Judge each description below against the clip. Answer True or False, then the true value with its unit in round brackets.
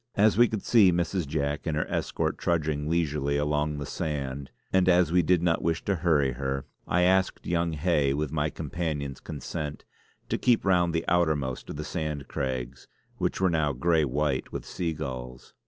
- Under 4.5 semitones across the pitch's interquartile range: True (3.4 semitones)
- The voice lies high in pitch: False (75 Hz)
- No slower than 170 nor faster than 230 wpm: True (185 wpm)